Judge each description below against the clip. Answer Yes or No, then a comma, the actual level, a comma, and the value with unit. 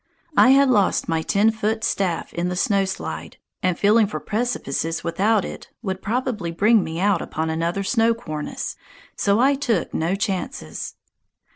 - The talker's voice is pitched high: Yes, high, 195 Hz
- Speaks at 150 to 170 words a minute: Yes, average, 160 wpm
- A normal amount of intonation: Yes, average, 4.9 semitones